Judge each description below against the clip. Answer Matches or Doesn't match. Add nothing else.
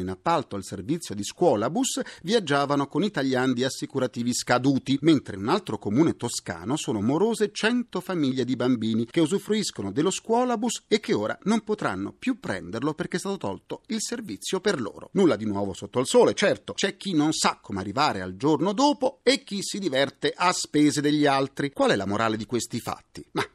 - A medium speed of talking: Doesn't match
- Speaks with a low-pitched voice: Doesn't match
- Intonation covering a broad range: Matches